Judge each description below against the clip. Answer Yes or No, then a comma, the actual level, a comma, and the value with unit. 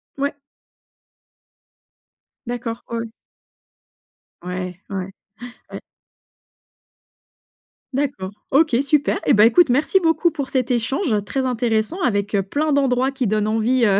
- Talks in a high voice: Yes, high, 245 Hz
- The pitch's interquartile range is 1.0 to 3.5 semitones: No, average, 4.7 semitones